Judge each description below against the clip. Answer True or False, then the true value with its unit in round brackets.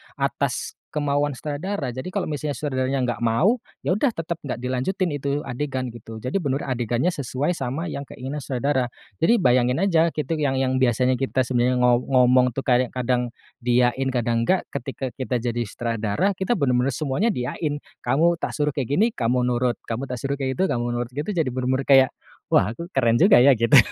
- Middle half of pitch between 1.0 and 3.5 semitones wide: True (3.2 semitones)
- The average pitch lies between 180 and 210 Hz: False (130 Hz)